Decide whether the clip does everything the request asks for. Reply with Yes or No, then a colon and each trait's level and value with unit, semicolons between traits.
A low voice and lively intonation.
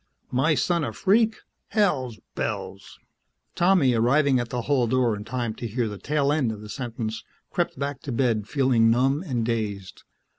No: low, 125 Hz; average, 4.0 semitones